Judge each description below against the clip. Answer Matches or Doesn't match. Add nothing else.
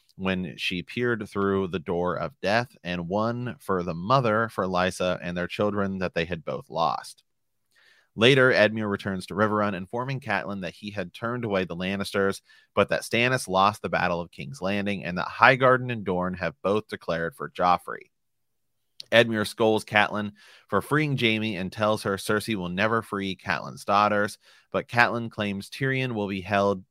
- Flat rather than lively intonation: Doesn't match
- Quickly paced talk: Doesn't match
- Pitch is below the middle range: Matches